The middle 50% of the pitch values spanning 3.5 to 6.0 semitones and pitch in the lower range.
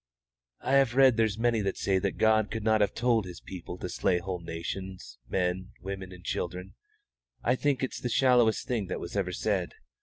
Yes: average, 4.0 semitones; low, 100 Hz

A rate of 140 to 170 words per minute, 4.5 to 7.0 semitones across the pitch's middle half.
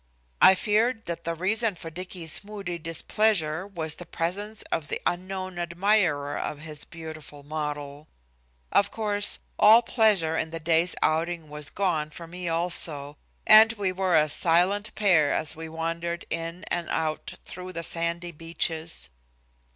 No: average, 150 wpm; average, 3.2 semitones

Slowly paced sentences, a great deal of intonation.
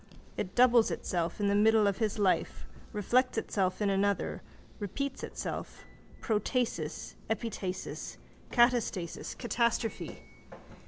No: slow, 105 wpm; average, 3.3 semitones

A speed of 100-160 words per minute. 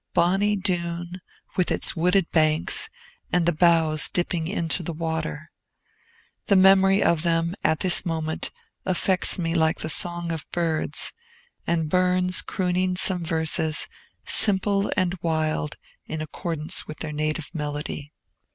Yes: slow, 135 wpm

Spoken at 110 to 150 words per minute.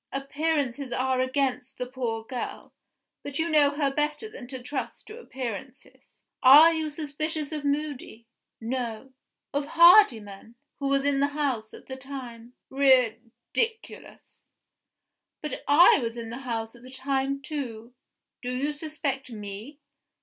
Yes: average, 140 wpm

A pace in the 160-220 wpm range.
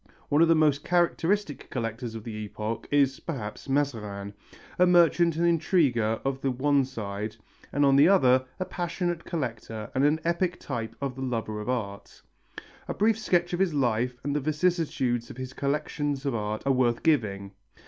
Yes: average, 180 wpm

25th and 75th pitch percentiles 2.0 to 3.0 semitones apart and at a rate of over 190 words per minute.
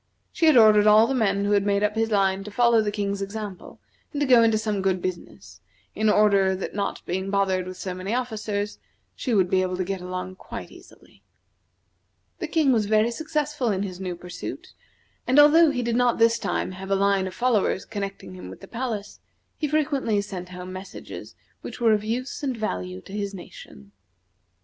No: average, 3.5 semitones; average, 200 wpm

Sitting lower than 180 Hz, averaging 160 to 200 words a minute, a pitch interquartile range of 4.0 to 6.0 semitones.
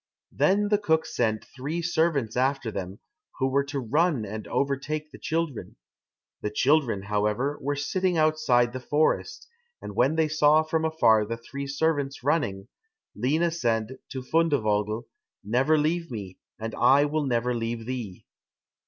No: medium, 140 Hz; average, 150 wpm; average, 5.3 semitones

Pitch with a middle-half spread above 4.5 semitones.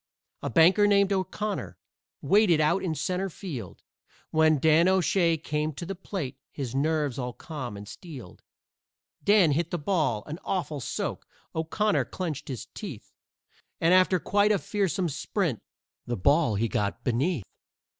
Yes: average, 5.2 semitones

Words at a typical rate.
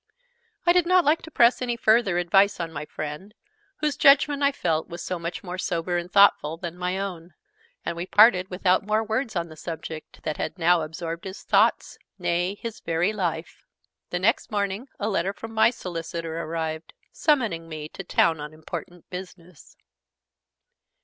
Yes: average, 175 wpm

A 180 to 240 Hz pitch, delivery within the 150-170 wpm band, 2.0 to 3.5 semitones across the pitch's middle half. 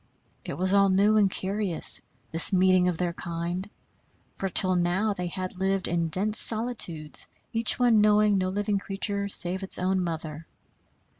Yes: high, 190 Hz; average, 160 wpm; narrow, 2.5 semitones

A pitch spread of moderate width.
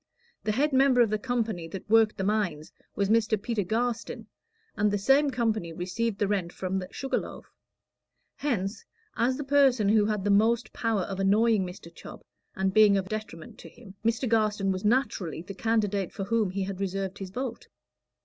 Yes: average, 3.1 semitones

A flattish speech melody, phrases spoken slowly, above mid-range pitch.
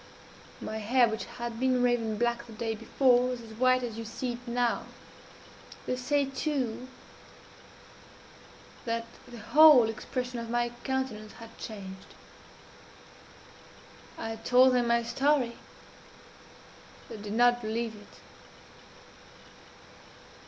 Yes: narrow, 2.1 semitones; slow, 115 wpm; high, 240 Hz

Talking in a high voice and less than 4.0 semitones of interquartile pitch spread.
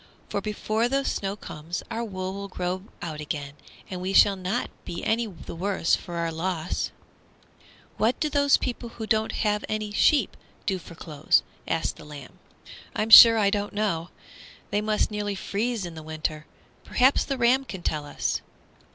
No: high, 200 Hz; average, 4.7 semitones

